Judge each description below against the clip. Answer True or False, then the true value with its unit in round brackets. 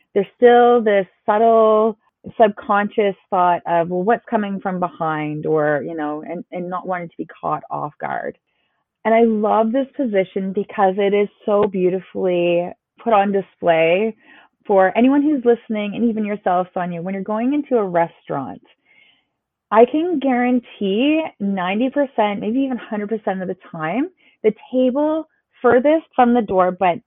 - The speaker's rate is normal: True (150 wpm)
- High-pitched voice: True (210 Hz)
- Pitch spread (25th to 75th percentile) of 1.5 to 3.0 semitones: False (4.8 semitones)